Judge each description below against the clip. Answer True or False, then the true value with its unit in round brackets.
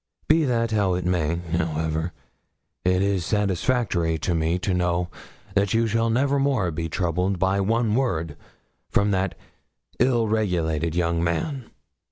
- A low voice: True (95 Hz)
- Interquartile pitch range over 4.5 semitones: True (5.0 semitones)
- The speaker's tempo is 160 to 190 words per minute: False (145 wpm)